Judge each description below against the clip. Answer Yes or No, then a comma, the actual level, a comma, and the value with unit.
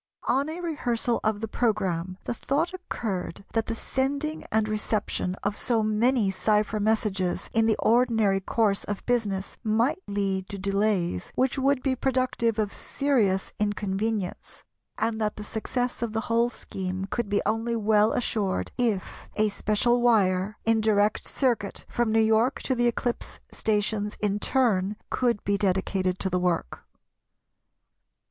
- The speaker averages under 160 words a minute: Yes, average, 150 wpm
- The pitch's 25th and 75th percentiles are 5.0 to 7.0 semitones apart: No, average, 3.1 semitones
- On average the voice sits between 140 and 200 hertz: No, high, 215 Hz